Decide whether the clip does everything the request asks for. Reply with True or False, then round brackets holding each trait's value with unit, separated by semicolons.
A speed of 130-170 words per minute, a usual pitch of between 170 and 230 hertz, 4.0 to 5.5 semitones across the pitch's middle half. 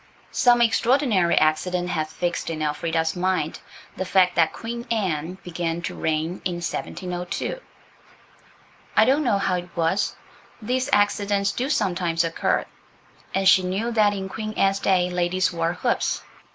False (145 wpm; 185 Hz; 3.2 semitones)